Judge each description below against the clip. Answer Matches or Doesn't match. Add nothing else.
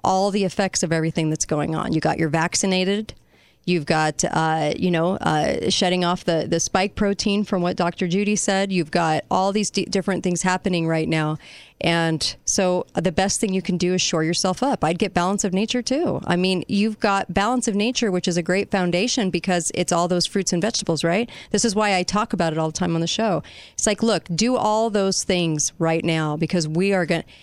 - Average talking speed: Doesn't match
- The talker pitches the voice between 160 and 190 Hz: Matches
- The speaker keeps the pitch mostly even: Doesn't match